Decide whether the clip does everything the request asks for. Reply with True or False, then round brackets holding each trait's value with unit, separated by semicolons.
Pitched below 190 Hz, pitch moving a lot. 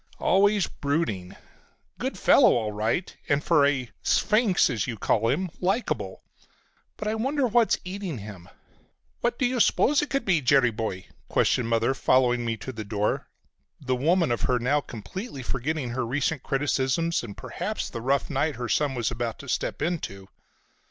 True (135 Hz; 7.2 semitones)